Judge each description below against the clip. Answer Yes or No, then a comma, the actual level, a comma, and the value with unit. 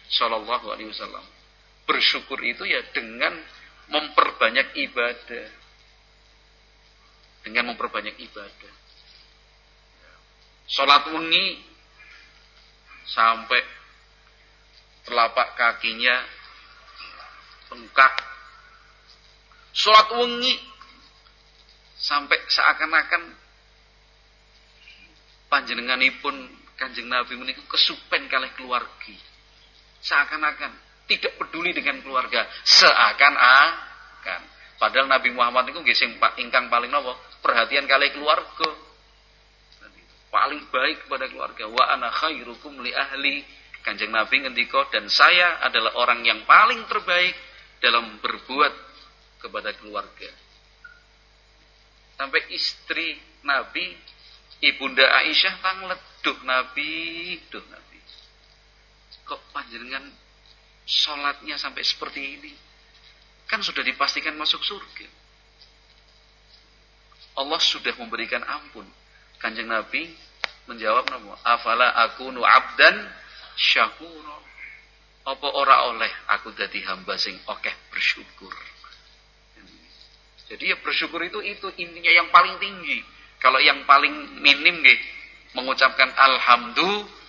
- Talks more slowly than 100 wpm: Yes, slow, 85 wpm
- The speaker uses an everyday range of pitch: No, wide, 5.8 semitones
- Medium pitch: Yes, medium, 145 Hz